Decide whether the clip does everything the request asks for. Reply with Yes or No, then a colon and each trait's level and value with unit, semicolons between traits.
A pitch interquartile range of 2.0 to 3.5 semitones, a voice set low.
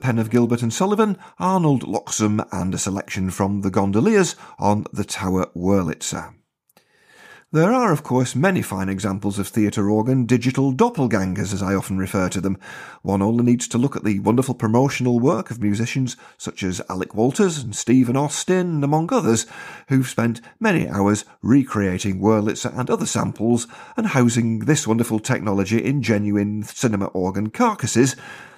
No: average, 4.6 semitones; low, 115 Hz